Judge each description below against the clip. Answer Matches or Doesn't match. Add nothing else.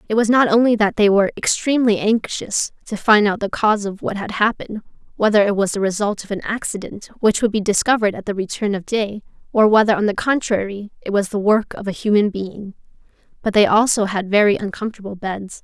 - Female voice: Matches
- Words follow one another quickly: Matches